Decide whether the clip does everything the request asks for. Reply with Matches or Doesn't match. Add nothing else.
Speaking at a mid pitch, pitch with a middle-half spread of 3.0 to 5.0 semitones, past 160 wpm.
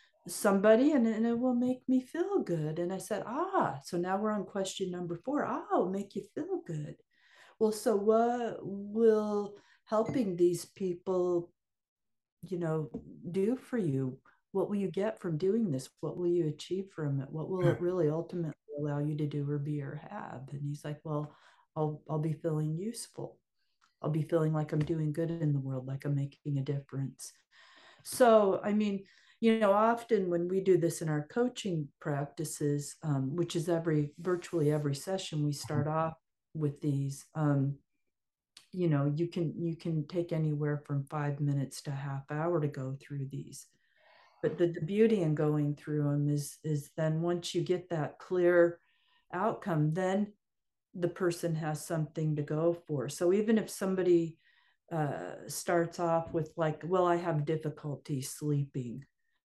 Matches